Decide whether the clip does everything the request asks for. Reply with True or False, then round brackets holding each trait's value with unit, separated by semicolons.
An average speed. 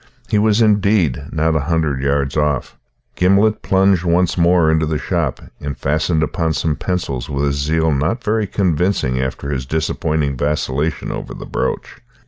True (160 wpm)